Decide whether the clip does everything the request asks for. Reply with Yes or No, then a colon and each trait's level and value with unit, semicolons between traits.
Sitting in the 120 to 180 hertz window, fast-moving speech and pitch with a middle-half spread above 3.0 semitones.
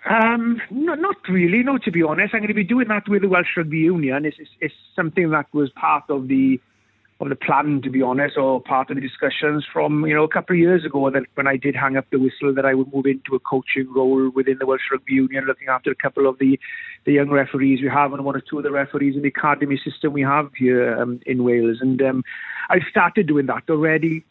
Yes: medium, 140 Hz; fast, 250 wpm; average, 3.5 semitones